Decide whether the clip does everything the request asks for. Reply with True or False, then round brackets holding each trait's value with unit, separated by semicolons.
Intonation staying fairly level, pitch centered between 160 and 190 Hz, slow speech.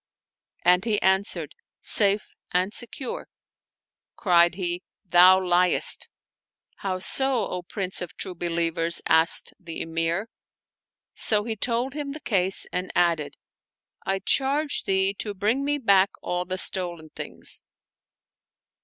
False (3.3 semitones; 185 Hz; 125 wpm)